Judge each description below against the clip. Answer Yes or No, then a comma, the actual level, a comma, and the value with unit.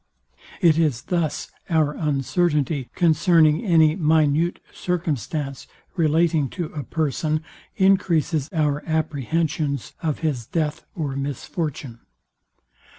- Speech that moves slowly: Yes, slow, 95 wpm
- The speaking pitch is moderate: Yes, medium, 155 Hz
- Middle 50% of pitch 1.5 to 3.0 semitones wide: Yes, narrow, 2.4 semitones